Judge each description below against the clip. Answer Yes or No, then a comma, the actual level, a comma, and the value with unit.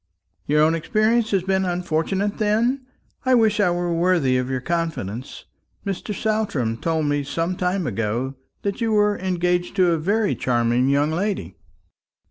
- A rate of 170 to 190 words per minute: No, average, 155 wpm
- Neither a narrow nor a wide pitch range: No, wide, 6.0 semitones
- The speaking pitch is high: No, medium, 175 Hz